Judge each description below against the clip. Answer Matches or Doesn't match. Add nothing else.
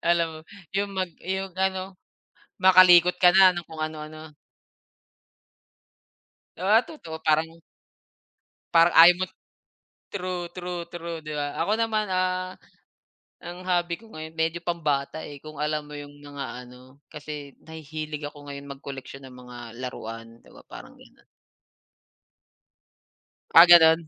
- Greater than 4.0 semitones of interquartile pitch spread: Doesn't match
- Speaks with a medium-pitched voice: Matches